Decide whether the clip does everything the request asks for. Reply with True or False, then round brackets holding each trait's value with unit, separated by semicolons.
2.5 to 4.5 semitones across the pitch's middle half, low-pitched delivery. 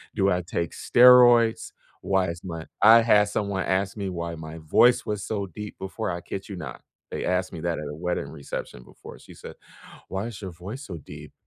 True (3.7 semitones; 95 Hz)